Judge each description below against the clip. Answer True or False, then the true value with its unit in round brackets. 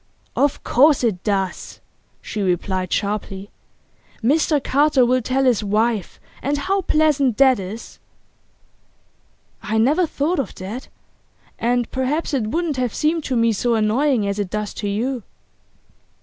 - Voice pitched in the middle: False (245 Hz)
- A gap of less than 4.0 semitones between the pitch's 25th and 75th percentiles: False (5.1 semitones)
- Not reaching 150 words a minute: True (140 wpm)